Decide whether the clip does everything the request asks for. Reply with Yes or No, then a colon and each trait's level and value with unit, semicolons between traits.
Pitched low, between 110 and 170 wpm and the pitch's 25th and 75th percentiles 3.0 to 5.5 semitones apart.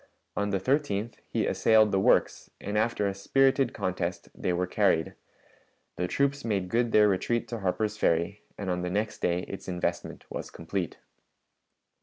Yes: low, 100 Hz; average, 165 wpm; average, 3.6 semitones